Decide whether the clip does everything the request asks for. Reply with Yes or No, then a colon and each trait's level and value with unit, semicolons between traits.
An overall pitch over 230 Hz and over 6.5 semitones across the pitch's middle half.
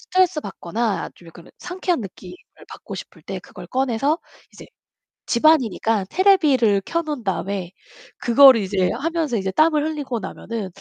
Yes: high, 240 Hz; wide, 7.8 semitones